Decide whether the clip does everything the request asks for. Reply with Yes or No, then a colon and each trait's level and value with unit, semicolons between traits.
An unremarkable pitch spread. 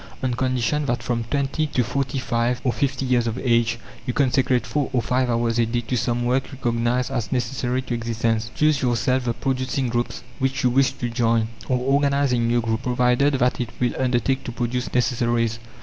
No: narrow, 1.9 semitones